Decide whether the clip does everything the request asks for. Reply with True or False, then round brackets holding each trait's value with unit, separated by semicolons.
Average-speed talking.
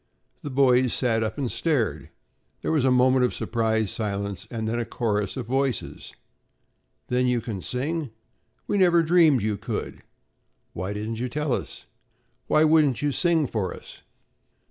True (160 wpm)